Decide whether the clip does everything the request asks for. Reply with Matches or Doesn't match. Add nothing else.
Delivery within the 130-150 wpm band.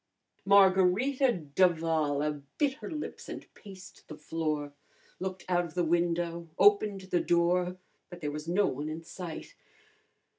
Matches